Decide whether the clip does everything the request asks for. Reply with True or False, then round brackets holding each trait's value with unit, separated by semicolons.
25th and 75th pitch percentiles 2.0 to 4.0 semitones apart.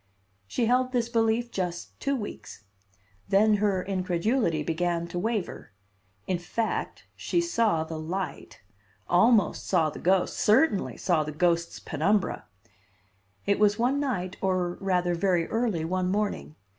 False (4.4 semitones)